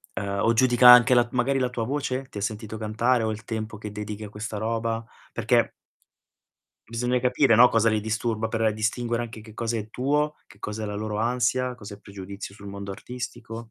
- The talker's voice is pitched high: No, low, 115 Hz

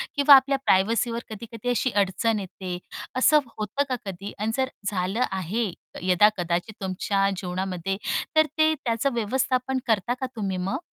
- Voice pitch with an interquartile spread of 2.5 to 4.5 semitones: No, average, 5.0 semitones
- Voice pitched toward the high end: Yes, high, 215 Hz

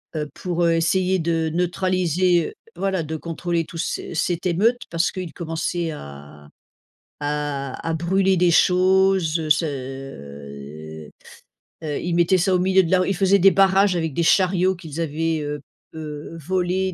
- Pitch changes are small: No, average, 3.5 semitones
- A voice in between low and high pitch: Yes, medium, 170 Hz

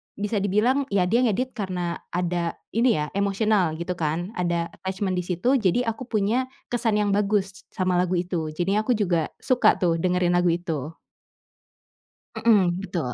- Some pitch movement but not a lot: Yes, average, 3.4 semitones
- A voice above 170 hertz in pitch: Yes, high, 190 Hz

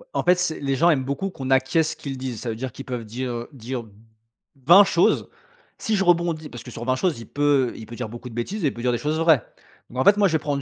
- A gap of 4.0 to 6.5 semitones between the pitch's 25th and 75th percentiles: Yes, average, 4.9 semitones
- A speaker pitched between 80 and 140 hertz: Yes, low, 135 Hz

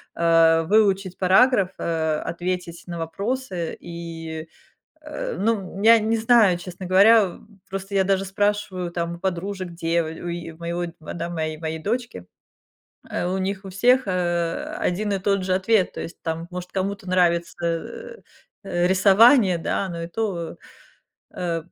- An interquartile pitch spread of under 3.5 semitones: Yes, average, 3.0 semitones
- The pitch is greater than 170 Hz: Yes, medium, 185 Hz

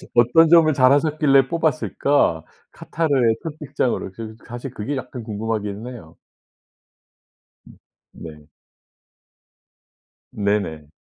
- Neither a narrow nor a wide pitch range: No, wide, 5.8 semitones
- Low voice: Yes, low, 125 Hz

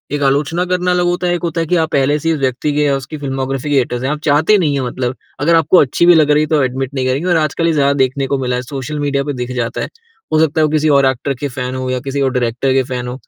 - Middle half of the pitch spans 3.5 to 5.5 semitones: No, average, 3.1 semitones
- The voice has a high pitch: No, medium, 140 Hz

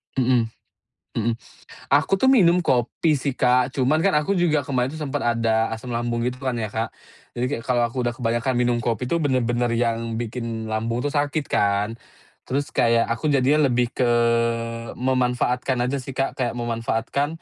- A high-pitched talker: No, low, 125 Hz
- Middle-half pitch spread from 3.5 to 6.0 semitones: No, average, 3.1 semitones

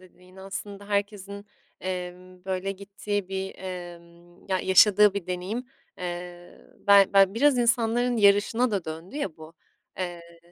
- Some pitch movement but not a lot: No, narrow, 2.3 semitones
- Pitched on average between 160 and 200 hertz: Yes, high, 190 Hz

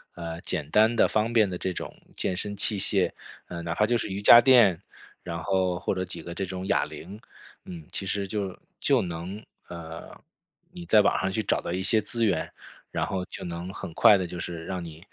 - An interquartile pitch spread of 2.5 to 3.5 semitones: Yes, average, 3.2 semitones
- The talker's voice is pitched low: Yes, very low, 95 Hz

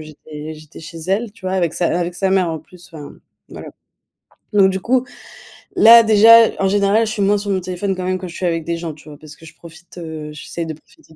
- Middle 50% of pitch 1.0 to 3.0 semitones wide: No, average, 3.8 semitones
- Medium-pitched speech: Yes, medium, 180 Hz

